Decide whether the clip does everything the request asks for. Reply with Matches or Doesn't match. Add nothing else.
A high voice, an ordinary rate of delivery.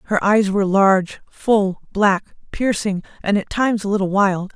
Matches